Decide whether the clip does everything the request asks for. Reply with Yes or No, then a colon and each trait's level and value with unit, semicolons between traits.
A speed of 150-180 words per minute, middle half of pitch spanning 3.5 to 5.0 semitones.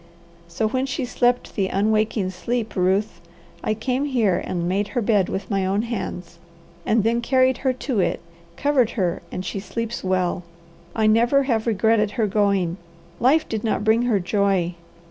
Yes: average, 170 wpm; average, 3.8 semitones